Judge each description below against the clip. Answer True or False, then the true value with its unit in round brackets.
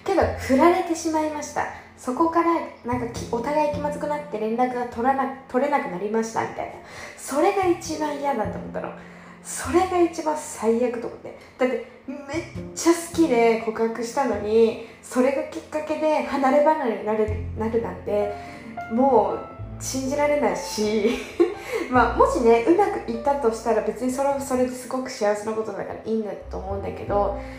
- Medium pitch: False (255 Hz)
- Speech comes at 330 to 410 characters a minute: True (350 characters per minute)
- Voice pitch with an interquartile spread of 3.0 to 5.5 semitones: True (5.2 semitones)